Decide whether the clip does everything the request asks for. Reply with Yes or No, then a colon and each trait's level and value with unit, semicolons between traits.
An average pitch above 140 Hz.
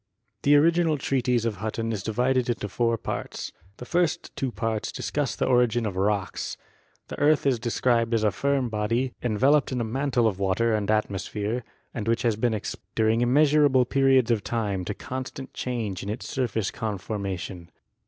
No: low, 115 Hz